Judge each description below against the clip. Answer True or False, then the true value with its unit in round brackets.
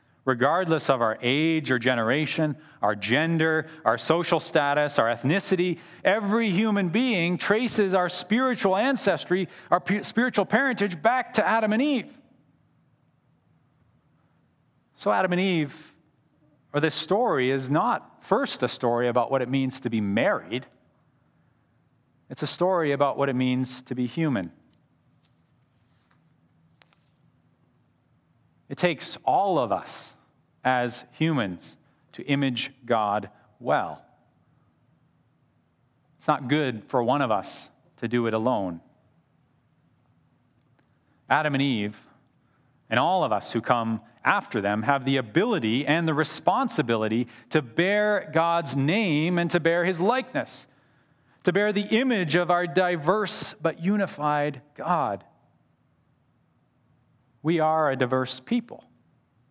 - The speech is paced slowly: True (120 wpm)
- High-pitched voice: False (150 Hz)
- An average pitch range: False (5.7 semitones)